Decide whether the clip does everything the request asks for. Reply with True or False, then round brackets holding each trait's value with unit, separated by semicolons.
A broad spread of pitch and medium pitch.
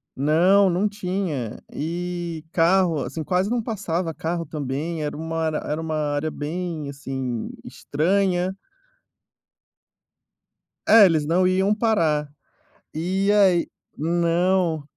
False (3.3 semitones; 170 Hz)